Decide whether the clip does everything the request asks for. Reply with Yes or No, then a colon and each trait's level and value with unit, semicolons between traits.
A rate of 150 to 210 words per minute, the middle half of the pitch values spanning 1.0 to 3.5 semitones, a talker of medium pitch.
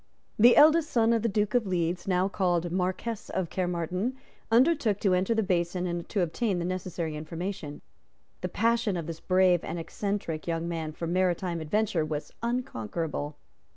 No: average, 165 wpm; average, 3.9 semitones; medium, 180 Hz